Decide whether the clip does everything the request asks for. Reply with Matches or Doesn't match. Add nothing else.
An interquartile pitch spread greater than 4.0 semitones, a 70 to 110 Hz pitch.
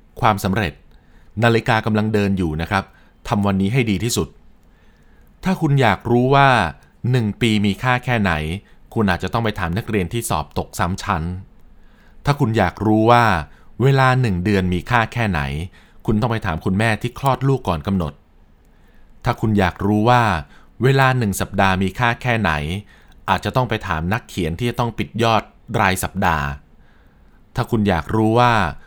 Matches